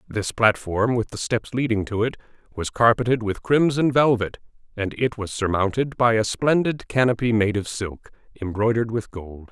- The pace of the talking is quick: No, average, 170 wpm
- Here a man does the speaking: Yes, male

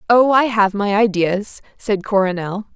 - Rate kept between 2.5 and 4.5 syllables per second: Yes, 4.3 syllables/s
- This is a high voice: Yes, high, 205 Hz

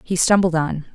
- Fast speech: No, average, 190 wpm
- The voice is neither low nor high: Yes, medium, 170 Hz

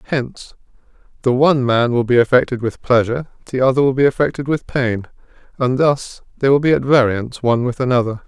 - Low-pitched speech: Yes, low, 130 Hz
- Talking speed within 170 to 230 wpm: Yes, average, 190 wpm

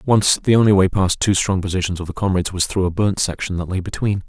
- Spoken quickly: Yes, fast, 265 wpm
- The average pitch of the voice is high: No, very low, 95 Hz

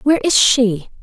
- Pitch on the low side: No, high, 240 Hz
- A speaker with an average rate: Yes, average, 175 wpm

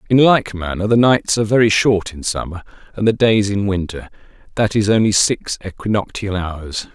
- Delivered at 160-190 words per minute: Yes, average, 180 wpm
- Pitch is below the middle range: Yes, low, 100 Hz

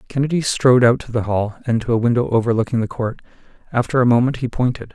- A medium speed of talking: No, fast, 220 wpm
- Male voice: Yes, male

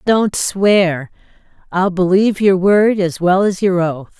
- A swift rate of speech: No, average, 155 wpm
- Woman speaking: Yes, female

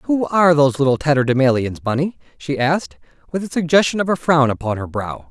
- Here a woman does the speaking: No, male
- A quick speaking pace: No, average, 190 wpm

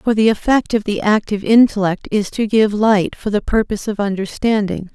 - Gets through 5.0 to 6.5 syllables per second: Yes, 5.4 syllables/s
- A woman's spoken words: Yes, female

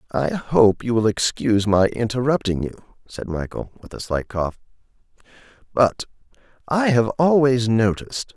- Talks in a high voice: No, low, 120 Hz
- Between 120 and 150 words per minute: Yes, slow, 135 wpm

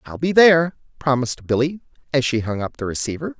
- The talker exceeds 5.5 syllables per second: Yes, 6.3 syllables/s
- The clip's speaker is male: Yes, male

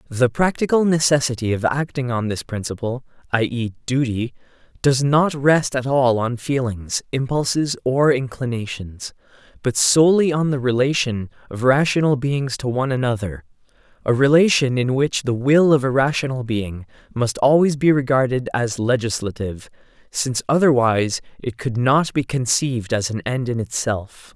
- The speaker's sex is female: No, male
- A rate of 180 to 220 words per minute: No, average, 150 wpm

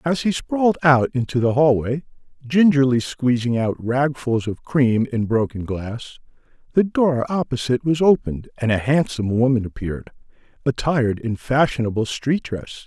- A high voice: No, low, 130 Hz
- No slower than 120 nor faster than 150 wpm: Yes, average, 145 wpm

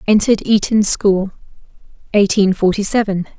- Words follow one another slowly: Yes, slow, 105 wpm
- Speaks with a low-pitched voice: No, high, 200 Hz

